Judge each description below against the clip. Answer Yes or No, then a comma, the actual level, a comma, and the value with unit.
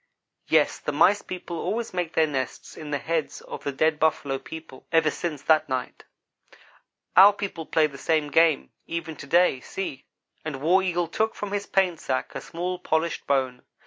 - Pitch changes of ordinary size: Yes, average, 3.6 semitones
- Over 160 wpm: Yes, average, 180 wpm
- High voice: No, medium, 160 Hz